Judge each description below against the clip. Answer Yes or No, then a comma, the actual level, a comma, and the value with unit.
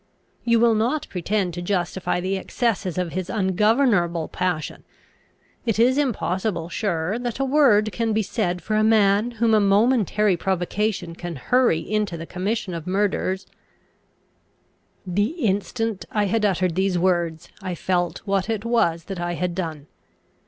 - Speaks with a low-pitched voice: No, high, 195 Hz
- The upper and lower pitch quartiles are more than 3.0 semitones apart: Yes, average, 3.9 semitones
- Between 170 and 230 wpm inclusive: No, average, 155 wpm